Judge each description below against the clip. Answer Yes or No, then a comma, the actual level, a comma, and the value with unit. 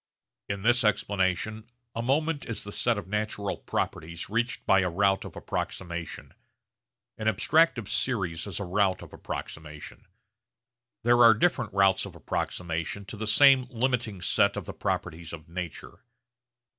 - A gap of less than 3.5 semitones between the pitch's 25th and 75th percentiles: No, average, 4.3 semitones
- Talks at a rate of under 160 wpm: Yes, average, 145 wpm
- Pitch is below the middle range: Yes, low, 100 Hz